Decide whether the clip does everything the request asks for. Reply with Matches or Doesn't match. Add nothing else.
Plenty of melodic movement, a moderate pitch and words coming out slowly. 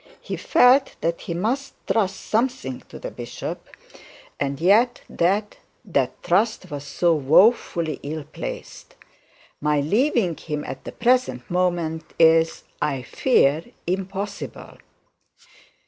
Matches